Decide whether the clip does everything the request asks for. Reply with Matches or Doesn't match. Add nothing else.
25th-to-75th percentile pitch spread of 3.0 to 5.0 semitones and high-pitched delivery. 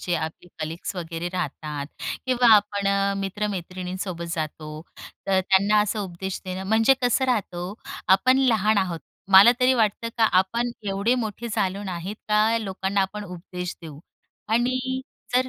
Matches